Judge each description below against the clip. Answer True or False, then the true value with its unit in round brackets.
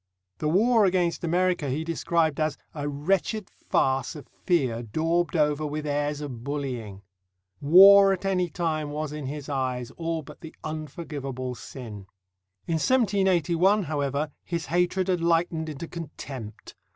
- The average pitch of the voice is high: False (155 Hz)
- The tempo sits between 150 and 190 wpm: False (140 wpm)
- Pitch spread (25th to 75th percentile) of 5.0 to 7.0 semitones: False (3.6 semitones)